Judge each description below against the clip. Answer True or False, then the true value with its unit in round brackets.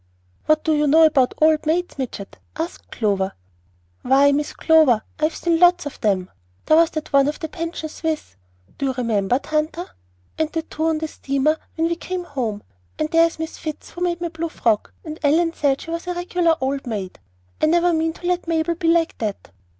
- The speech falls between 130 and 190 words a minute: False (200 wpm)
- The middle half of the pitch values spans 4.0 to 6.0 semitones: False (3.3 semitones)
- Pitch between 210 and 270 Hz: False (315 Hz)